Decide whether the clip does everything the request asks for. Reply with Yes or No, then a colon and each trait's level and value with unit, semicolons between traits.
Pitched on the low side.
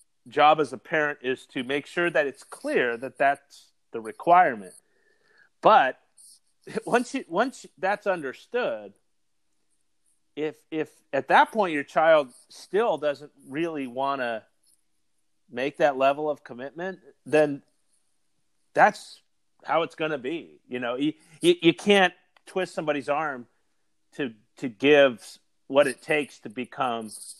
No: medium, 150 Hz